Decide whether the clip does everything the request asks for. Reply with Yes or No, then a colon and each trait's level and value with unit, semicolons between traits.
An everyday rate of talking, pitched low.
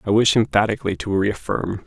Yes: average, 160 wpm; low, 105 Hz